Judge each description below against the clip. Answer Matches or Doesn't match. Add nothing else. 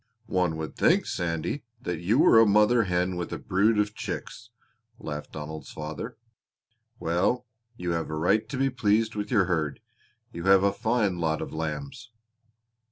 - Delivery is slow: Doesn't match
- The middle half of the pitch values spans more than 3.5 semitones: Matches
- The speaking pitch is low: Matches